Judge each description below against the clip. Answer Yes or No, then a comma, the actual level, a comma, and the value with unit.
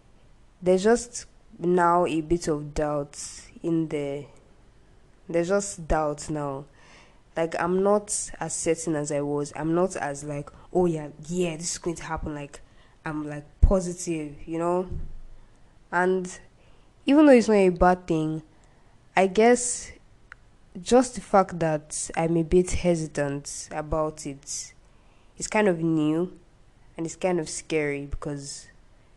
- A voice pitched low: No, medium, 160 Hz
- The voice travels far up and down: No, average, 3.8 semitones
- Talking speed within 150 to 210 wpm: No, average, 140 wpm